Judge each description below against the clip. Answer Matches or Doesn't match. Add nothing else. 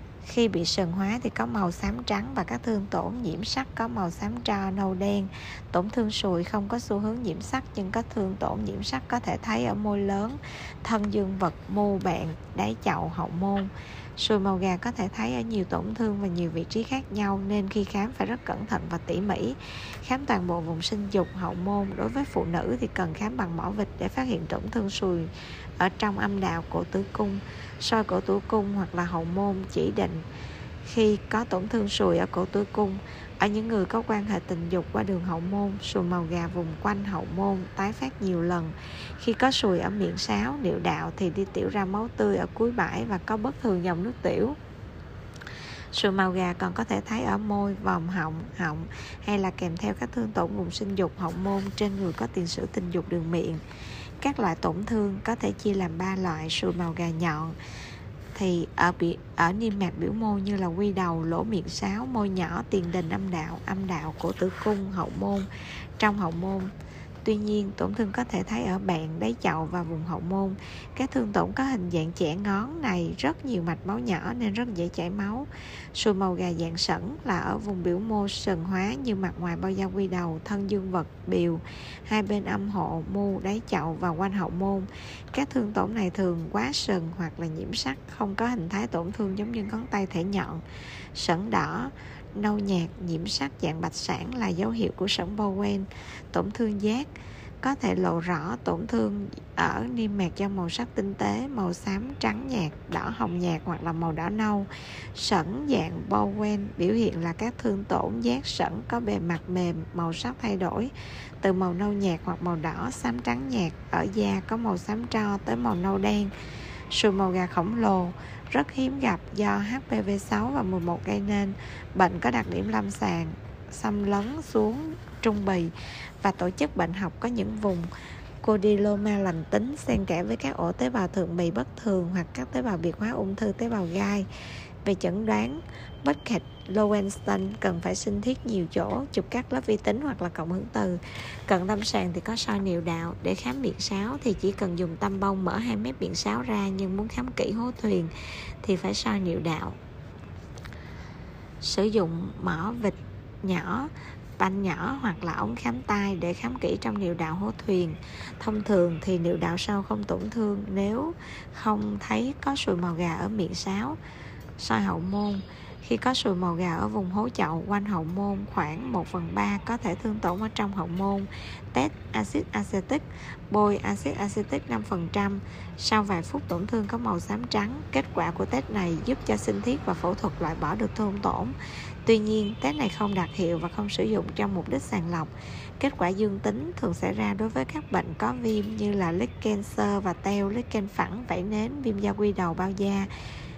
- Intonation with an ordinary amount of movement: Matches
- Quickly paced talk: Doesn't match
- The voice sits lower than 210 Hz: Matches